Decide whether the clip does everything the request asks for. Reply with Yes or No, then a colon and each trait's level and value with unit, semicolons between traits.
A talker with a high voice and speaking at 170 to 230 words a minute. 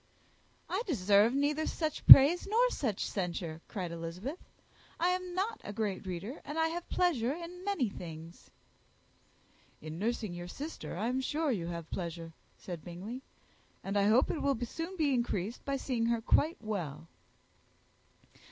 No: high, 235 Hz; average, 155 wpm